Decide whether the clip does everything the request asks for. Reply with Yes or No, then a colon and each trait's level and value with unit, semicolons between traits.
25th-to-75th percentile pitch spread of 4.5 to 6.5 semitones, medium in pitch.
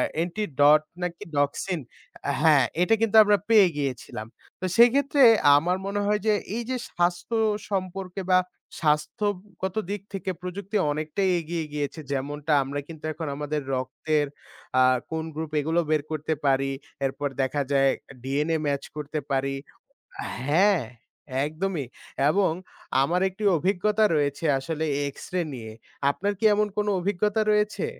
Yes: average, 5.3 semitones; medium, 165 Hz